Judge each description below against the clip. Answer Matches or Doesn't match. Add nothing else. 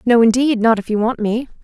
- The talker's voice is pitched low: Doesn't match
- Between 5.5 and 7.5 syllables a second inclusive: Matches